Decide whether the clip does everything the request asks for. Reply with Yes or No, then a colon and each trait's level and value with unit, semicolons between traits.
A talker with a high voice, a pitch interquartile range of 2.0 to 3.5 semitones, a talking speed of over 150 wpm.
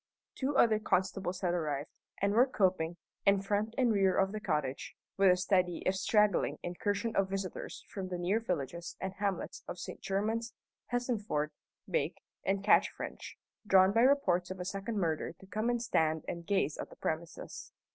Yes: high, 195 Hz; average, 3.2 semitones; average, 175 wpm